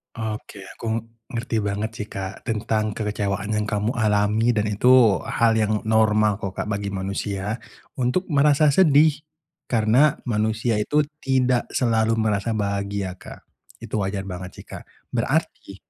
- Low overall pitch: Yes, low, 110 Hz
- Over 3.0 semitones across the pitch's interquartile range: No, narrow, 2.5 semitones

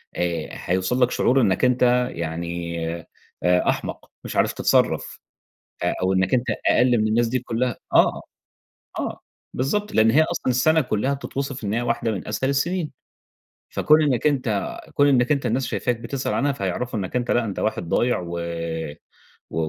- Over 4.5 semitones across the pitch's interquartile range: Yes, wide, 5.4 semitones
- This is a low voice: Yes, low, 120 Hz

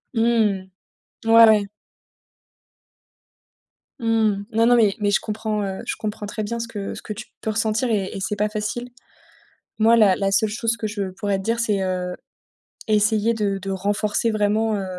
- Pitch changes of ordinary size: No, narrow, 2.0 semitones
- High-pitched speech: Yes, high, 210 Hz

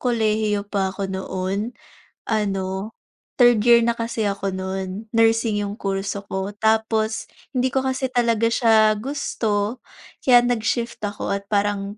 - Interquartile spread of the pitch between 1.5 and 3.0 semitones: Yes, average, 2.7 semitones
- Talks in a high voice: Yes, high, 215 Hz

